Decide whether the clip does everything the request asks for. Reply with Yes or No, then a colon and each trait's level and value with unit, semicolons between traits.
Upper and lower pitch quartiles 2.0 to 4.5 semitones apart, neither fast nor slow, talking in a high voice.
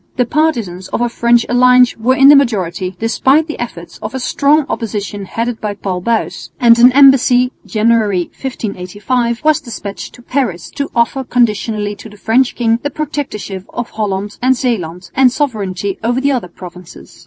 Yes: average, 4.0 semitones; average, 170 wpm; high, 235 Hz